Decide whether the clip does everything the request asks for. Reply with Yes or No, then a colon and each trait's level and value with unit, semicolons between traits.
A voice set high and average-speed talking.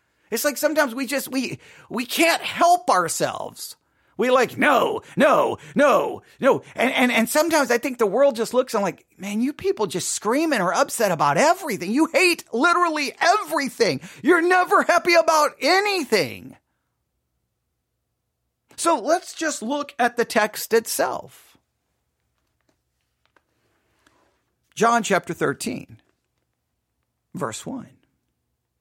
No: very high, 280 Hz; slow, 125 wpm